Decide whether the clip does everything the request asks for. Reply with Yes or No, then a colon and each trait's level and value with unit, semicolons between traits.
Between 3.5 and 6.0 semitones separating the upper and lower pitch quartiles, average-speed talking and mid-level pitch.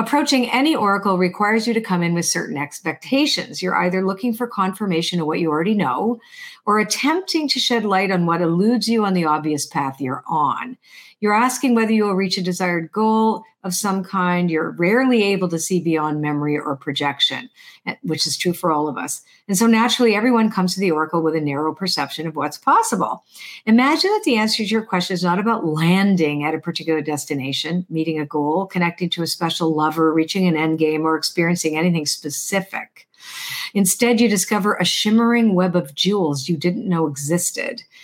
Yes: wide, 5.6 semitones; average, 190 wpm; medium, 180 Hz